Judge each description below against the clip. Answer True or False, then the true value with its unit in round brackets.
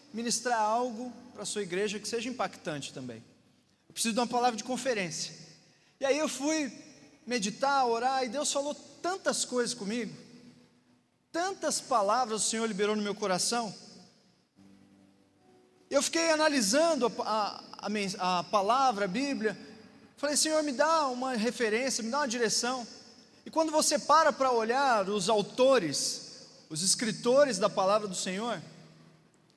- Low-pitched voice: False (235 Hz)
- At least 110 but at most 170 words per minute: True (140 wpm)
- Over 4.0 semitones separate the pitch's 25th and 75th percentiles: True (4.9 semitones)